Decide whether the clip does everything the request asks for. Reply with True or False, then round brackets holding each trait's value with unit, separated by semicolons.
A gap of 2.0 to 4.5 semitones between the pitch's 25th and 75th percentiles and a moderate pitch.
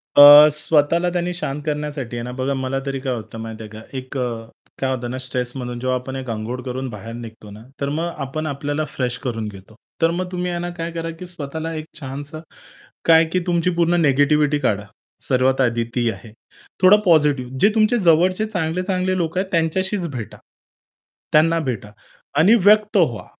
False (5.2 semitones; 145 Hz)